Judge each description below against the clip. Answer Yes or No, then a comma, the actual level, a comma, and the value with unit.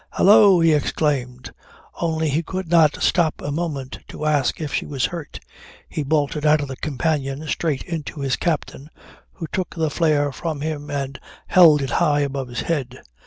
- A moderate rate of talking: Yes, average, 175 wpm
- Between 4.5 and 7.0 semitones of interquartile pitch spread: No, average, 2.8 semitones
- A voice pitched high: No, medium, 150 Hz